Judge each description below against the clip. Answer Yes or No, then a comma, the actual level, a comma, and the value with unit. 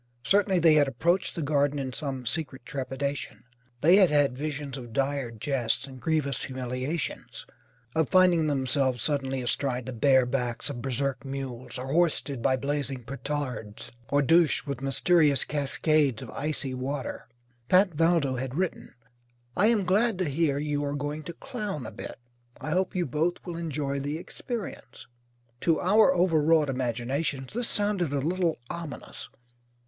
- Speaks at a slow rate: No, average, 155 wpm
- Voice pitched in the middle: Yes, medium, 145 Hz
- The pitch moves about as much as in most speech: Yes, average, 3.9 semitones